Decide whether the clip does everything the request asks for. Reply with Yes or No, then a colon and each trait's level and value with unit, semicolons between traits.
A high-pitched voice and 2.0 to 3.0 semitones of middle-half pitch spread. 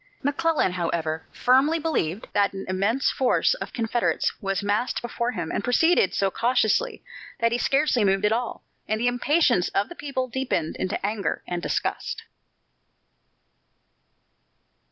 No: high, 230 Hz; average, 5.2 semitones